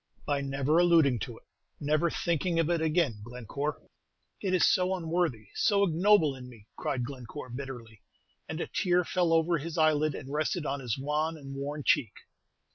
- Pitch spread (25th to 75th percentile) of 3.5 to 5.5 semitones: Yes, average, 3.9 semitones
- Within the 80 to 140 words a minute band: No, average, 175 wpm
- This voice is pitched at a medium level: Yes, medium, 150 Hz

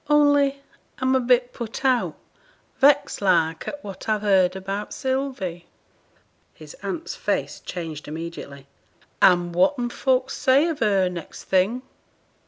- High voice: Yes, high, 220 Hz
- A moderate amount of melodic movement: No, wide, 6.7 semitones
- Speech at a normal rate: No, slow, 130 wpm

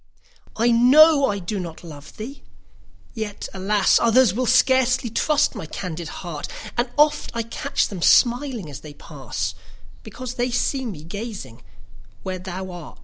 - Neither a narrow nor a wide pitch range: No, wide, 6.6 semitones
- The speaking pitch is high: Yes, high, 220 Hz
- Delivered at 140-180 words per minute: Yes, average, 145 wpm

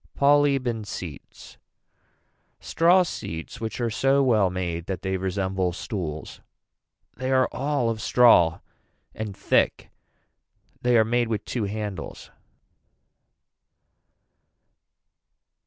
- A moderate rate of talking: No, slow, 105 wpm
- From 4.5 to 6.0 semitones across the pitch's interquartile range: Yes, average, 5.2 semitones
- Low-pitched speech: Yes, low, 110 Hz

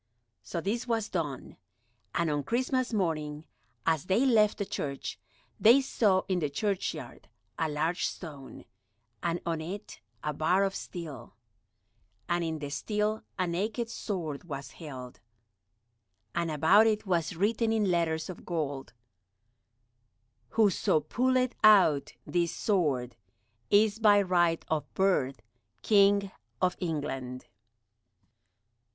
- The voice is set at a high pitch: No, medium, 175 Hz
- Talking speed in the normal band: No, slow, 120 wpm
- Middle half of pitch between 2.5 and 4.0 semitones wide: No, average, 5.2 semitones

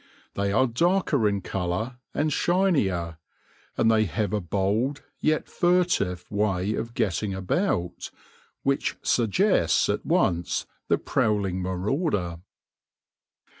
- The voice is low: Yes, low, 105 Hz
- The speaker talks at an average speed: No, slow, 110 wpm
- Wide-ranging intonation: Yes, wide, 6.9 semitones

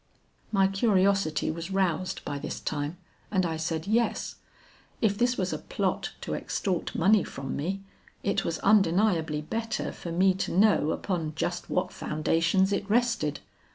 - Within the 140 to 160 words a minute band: Yes, average, 155 wpm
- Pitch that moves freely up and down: No, average, 3.8 semitones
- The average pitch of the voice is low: No, medium, 185 Hz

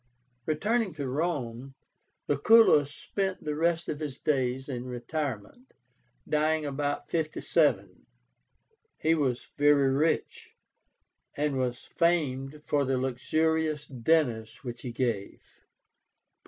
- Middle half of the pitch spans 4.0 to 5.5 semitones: No, average, 3.6 semitones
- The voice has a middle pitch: Yes, medium, 145 Hz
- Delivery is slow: Yes, slow, 105 wpm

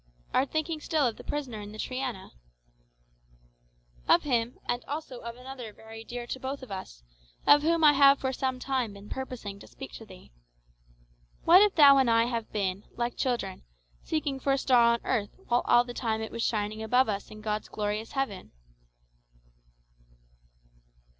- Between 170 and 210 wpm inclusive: Yes, average, 180 wpm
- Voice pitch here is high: Yes, high, 240 Hz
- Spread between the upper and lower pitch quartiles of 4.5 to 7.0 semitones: No, average, 3.8 semitones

